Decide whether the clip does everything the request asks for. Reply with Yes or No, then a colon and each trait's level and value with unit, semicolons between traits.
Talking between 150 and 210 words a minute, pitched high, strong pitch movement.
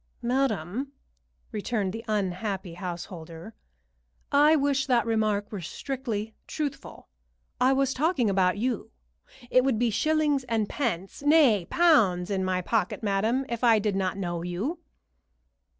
No: slow, 135 wpm; high, 220 Hz; wide, 5.8 semitones